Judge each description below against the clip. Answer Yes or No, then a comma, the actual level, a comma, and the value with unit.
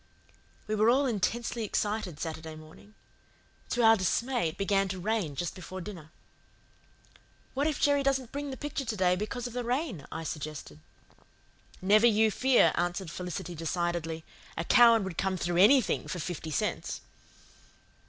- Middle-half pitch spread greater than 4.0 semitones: Yes, wide, 5.6 semitones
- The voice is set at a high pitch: Yes, high, 200 Hz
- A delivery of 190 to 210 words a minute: No, average, 155 wpm